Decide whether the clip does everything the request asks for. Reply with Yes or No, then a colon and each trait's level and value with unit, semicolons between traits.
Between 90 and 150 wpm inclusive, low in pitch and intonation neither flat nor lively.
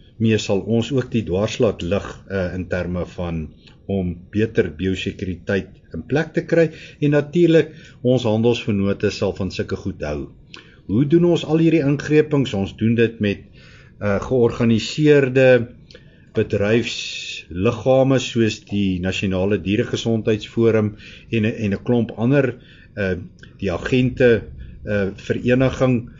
Yes: slow, 125 wpm; low, 115 Hz; average, 4.7 semitones